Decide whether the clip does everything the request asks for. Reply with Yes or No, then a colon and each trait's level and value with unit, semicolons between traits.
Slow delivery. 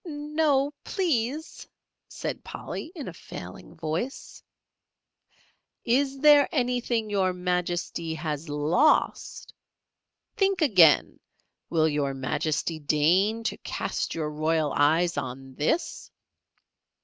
Yes: slow, 100 wpm